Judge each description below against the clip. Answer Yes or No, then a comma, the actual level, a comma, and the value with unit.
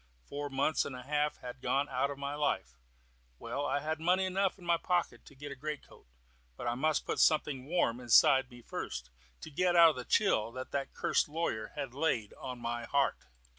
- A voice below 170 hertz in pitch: Yes, medium, 140 Hz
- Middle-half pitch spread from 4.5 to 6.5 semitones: No, average, 3.8 semitones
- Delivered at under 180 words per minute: No, average, 200 wpm